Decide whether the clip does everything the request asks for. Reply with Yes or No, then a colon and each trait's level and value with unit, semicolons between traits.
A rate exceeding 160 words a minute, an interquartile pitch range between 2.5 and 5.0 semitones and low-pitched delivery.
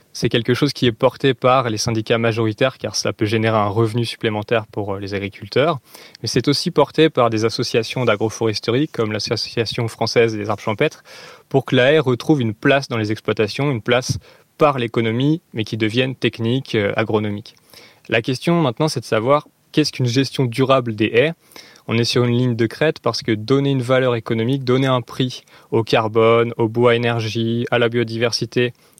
Yes: average, 185 wpm; average, 2.9 semitones; low, 120 Hz